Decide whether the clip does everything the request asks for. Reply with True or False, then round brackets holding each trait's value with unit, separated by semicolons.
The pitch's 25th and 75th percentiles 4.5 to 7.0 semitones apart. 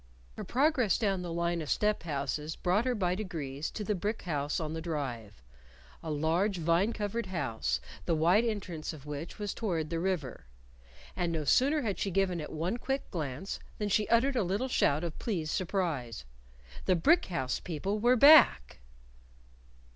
True (5.3 semitones)